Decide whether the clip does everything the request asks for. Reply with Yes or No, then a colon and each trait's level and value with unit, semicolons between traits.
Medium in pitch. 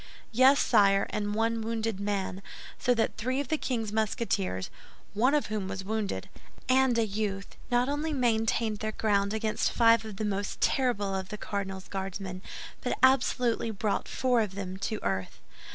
No: high, 215 Hz